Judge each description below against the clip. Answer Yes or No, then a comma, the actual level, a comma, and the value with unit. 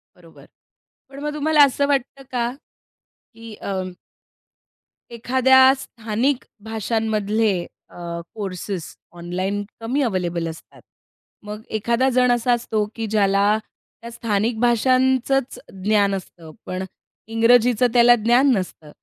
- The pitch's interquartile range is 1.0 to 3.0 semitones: No, average, 3.7 semitones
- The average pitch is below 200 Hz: No, high, 225 Hz